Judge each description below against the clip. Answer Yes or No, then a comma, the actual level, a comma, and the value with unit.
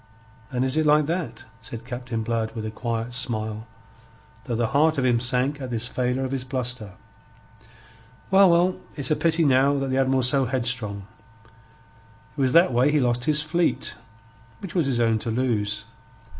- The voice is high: No, low, 130 Hz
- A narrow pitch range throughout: No, average, 3.4 semitones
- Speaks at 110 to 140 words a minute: No, average, 180 wpm